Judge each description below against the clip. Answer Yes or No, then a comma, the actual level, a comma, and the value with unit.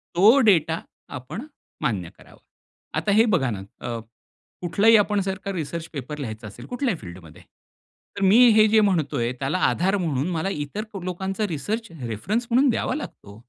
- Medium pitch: Yes, medium, 175 Hz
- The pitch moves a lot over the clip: Yes, wide, 7.6 semitones